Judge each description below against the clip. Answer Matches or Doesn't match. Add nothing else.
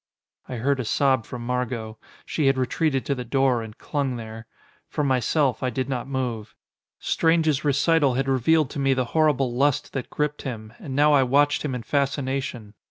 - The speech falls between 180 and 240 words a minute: Matches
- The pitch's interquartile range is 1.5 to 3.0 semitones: Matches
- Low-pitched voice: Matches